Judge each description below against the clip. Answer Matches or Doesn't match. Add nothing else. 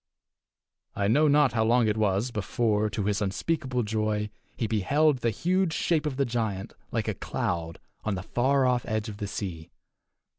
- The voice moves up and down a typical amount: Matches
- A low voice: Matches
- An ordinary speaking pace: Matches